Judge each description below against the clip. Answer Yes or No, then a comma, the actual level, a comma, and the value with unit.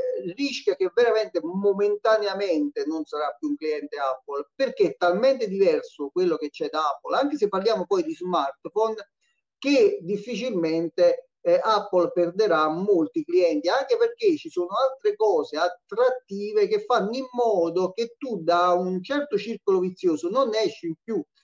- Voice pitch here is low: No, high, 220 Hz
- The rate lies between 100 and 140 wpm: No, average, 150 wpm